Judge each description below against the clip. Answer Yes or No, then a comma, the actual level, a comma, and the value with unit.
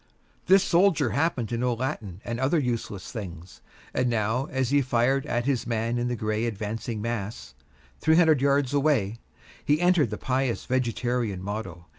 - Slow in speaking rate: No, average, 165 wpm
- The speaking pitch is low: Yes, low, 120 Hz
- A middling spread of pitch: Yes, average, 4.0 semitones